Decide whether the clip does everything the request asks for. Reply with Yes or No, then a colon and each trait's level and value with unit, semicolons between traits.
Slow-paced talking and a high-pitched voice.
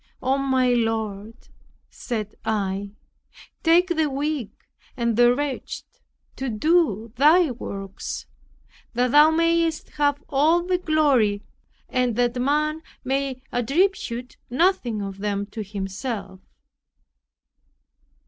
Yes: slow, 105 wpm; very high, 255 Hz